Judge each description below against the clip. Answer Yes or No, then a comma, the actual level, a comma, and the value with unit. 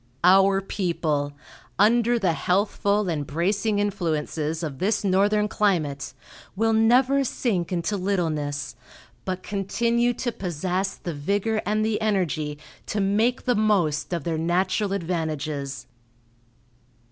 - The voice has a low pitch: No, high, 190 Hz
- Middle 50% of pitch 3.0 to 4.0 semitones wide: No, average, 4.7 semitones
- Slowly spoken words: Yes, slow, 120 wpm